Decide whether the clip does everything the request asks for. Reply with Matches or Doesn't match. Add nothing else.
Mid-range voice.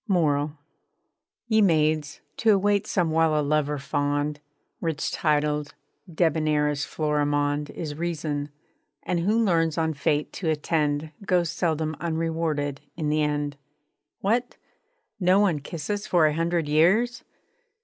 Matches